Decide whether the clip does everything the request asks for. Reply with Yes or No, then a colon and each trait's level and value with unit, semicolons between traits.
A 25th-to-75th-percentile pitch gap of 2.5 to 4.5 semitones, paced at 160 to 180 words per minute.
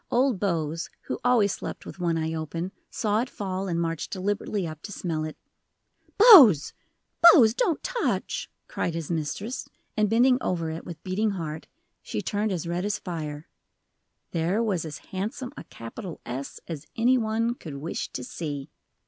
No: wide, 5.4 semitones; average, 165 wpm